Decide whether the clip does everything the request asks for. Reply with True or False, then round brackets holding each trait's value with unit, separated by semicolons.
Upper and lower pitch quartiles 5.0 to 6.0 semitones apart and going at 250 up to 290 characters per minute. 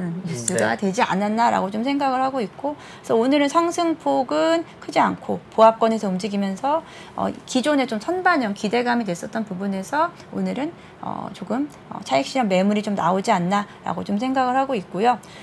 False (5.5 semitones; 355 characters per minute)